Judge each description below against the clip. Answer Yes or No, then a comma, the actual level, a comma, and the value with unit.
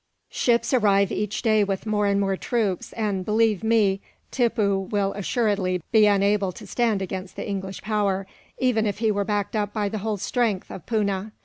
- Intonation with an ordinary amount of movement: No, narrow, 2.0 semitones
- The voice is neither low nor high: No, high, 205 Hz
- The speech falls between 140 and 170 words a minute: No, average, 185 wpm